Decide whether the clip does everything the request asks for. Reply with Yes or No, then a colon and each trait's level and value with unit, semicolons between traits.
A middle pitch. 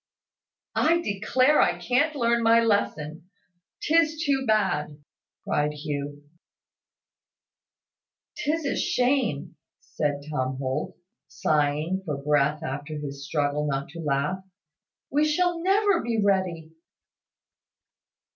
Yes: medium, 175 Hz